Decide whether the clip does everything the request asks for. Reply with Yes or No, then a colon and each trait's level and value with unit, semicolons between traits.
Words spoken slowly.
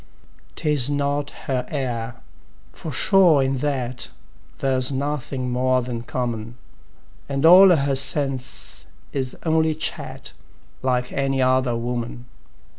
Yes: slow, 115 wpm